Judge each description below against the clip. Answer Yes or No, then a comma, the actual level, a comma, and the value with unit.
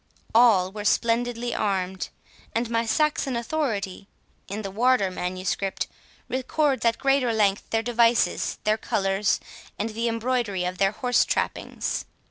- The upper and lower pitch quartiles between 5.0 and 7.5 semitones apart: No, average, 3.7 semitones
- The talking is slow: Yes, slow, 130 wpm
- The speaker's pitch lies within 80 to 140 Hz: No, high, 225 Hz